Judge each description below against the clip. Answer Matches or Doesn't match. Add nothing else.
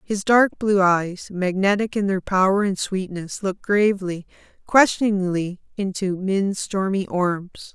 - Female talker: Matches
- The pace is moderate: Doesn't match